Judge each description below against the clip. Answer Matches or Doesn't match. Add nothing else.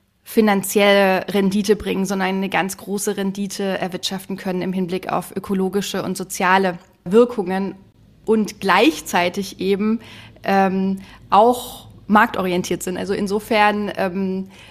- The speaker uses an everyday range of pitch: Doesn't match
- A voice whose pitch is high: Matches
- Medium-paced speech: Doesn't match